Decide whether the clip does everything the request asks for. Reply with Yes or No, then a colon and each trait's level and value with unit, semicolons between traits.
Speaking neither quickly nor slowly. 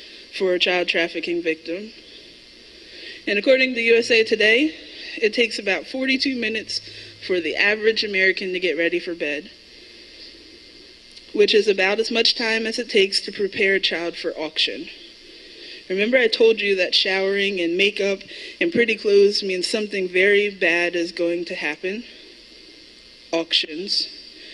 Yes: average, 145 wpm